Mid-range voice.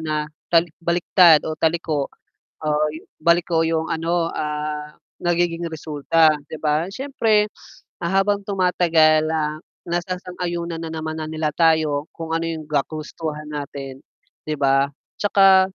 Yes: medium, 160 Hz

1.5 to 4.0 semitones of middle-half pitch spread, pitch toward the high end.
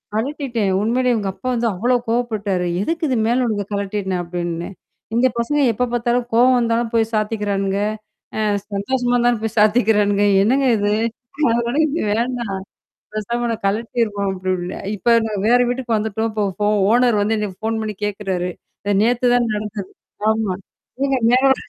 Yes: average, 3.0 semitones; high, 225 Hz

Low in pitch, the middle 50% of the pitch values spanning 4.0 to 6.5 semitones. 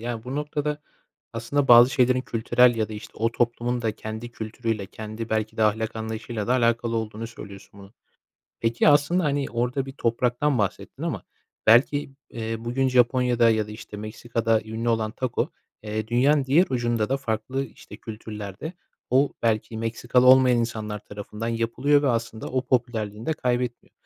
No: low, 115 Hz; narrow, 2.5 semitones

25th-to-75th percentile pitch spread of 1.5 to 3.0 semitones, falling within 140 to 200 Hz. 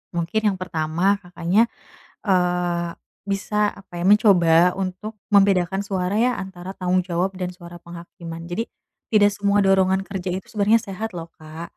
Yes: narrow, 2.4 semitones; medium, 185 Hz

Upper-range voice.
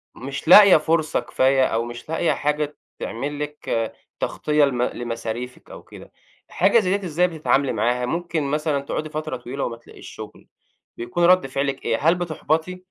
No: medium, 150 Hz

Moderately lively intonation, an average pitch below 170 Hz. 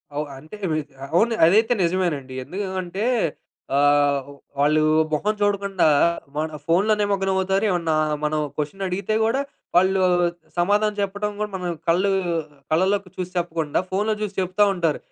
No: average, 4.1 semitones; medium, 185 Hz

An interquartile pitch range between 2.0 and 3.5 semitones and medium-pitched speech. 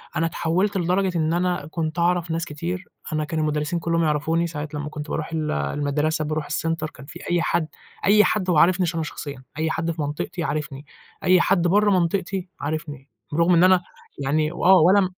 Yes: average, 2.7 semitones; medium, 165 Hz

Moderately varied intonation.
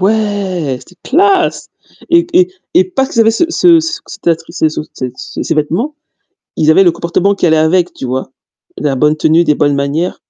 No: wide, 8.0 semitones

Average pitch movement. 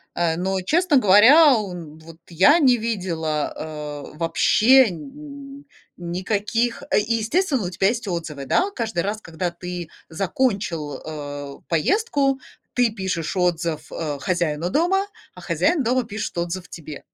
No: wide, 6.9 semitones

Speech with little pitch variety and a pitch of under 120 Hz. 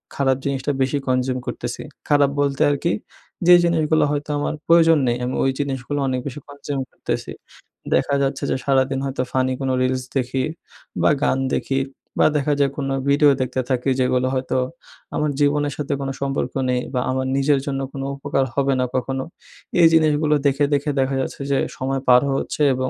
No: narrow, 1.8 semitones; low, 135 Hz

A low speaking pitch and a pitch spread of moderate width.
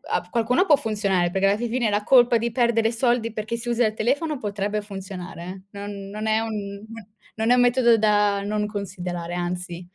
No: high, 210 Hz; average, 3.1 semitones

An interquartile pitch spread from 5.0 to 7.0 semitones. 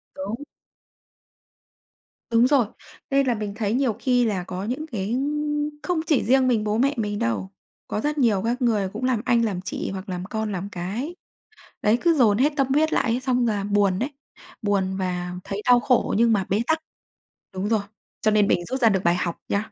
No: average, 4.3 semitones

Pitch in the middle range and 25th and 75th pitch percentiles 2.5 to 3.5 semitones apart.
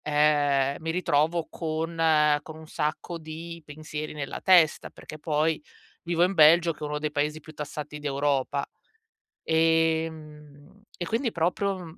No: medium, 155 Hz; narrow, 1.7 semitones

